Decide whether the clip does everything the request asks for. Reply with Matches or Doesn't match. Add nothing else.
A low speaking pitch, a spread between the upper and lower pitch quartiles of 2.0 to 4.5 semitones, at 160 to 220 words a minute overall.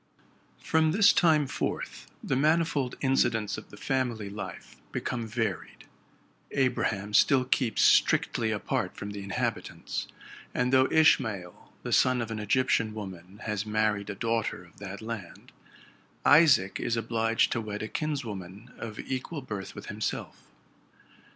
Doesn't match